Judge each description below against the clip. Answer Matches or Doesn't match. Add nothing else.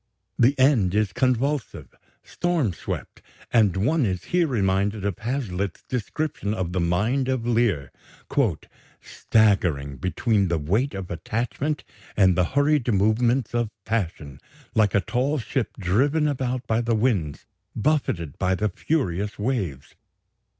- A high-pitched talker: Doesn't match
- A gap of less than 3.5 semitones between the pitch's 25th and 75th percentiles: Doesn't match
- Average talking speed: Doesn't match